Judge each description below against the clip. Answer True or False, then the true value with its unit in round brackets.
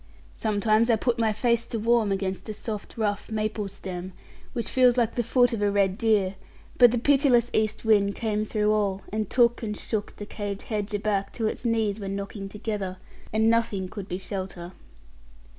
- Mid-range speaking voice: False (215 Hz)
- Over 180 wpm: True (190 wpm)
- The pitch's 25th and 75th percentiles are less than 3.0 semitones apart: True (2.4 semitones)